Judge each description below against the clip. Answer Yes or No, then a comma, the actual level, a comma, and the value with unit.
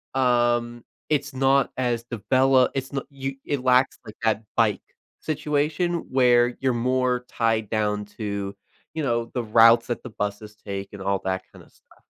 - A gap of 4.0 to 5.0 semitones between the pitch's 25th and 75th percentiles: No, average, 3.6 semitones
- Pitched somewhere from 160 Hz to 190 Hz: No, low, 120 Hz